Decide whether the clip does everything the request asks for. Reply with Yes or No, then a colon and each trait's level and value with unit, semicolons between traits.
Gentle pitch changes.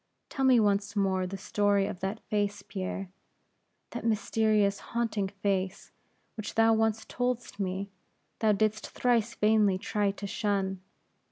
Yes: narrow, 2.0 semitones